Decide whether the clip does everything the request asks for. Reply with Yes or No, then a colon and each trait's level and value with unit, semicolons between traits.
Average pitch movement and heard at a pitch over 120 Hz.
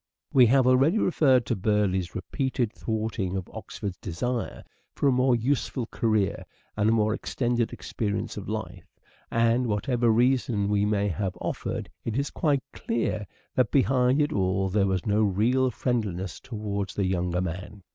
No: average, 4.1 semitones; low, 110 Hz